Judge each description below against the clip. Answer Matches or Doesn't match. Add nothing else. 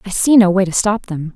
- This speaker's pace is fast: Matches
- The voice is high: Matches